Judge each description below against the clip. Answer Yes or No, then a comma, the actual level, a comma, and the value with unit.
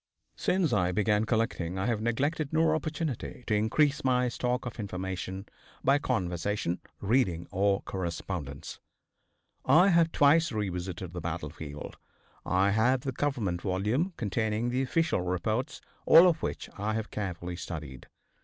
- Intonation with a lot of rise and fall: Yes, wide, 6.5 semitones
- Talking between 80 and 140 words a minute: Yes, slow, 135 wpm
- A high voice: No, low, 105 Hz